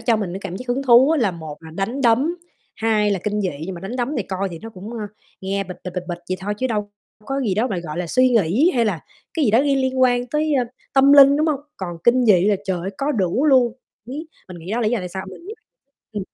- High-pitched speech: Yes, high, 220 Hz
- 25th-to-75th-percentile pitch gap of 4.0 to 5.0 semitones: No, wide, 5.4 semitones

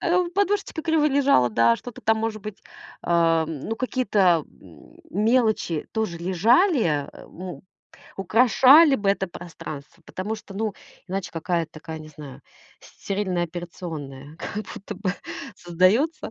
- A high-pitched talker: Yes, high, 195 Hz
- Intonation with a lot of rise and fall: Yes, wide, 5.7 semitones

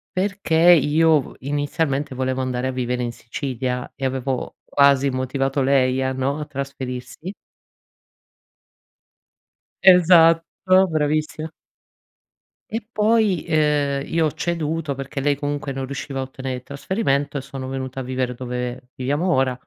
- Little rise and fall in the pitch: No, average, 3.0 semitones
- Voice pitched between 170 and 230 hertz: No, medium, 140 Hz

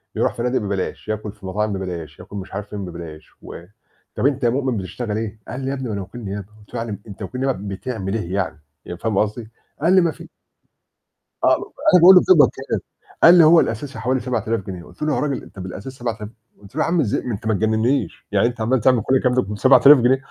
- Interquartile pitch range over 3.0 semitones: Yes, average, 4.7 semitones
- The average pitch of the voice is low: Yes, low, 110 Hz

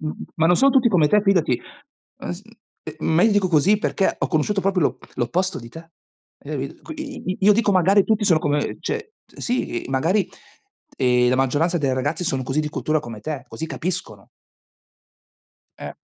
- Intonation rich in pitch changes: Yes, wide, 5.8 semitones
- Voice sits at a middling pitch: Yes, medium, 165 Hz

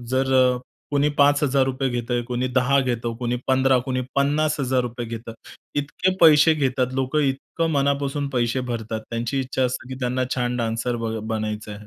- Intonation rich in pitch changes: No, narrow, 2.5 semitones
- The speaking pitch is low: Yes, low, 130 Hz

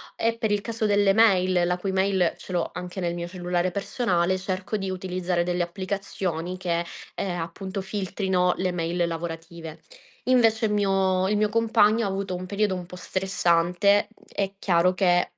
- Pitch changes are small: Yes, narrow, 2.2 semitones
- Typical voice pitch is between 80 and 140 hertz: No, medium, 185 Hz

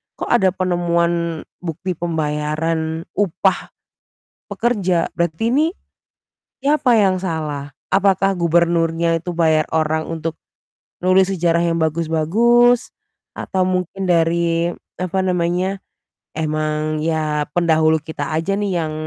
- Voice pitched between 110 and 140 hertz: No, medium, 170 Hz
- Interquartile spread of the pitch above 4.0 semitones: No, average, 2.7 semitones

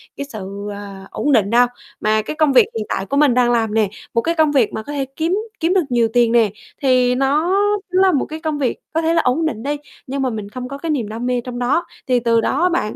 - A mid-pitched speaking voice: No, very high, 250 Hz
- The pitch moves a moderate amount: Yes, average, 4.7 semitones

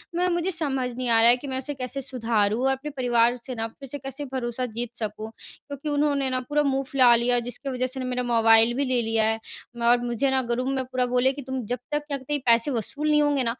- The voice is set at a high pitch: Yes, very high, 255 Hz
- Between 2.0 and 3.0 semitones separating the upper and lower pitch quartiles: Yes, narrow, 2.5 semitones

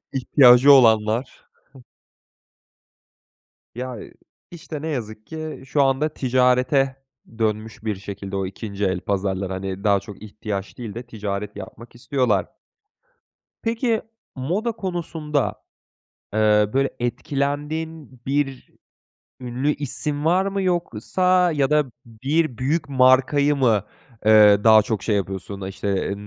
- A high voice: No, low, 125 Hz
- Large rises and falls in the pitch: Yes, wide, 5.7 semitones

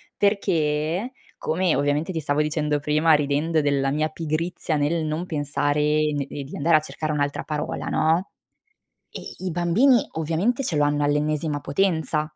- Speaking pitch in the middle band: Yes, medium, 155 Hz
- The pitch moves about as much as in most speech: No, narrow, 2.3 semitones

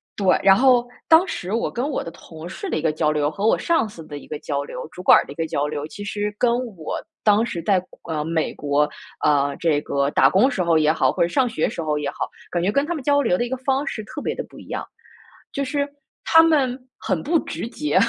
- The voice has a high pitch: Yes, high, 195 Hz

